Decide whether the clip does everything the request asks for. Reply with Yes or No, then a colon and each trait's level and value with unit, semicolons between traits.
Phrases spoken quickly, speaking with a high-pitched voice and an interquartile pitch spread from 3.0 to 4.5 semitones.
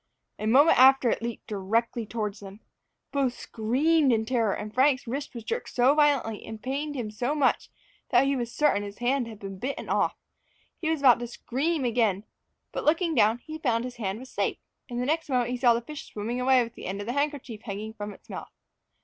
Yes: fast, 215 wpm; high, 245 Hz; average, 4.0 semitones